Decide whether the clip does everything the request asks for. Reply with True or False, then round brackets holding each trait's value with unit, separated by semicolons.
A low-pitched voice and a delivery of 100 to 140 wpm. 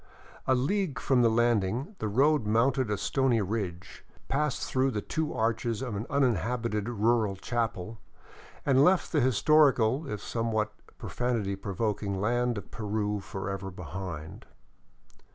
True (115 Hz; 135 wpm)